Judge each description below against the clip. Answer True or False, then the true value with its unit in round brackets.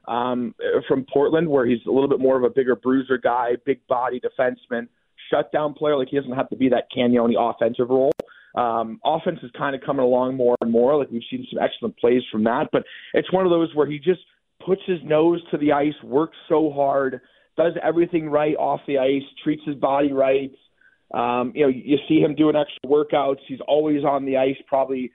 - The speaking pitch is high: False (135 Hz)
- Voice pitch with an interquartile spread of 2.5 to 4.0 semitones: True (3.2 semitones)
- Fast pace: True (210 wpm)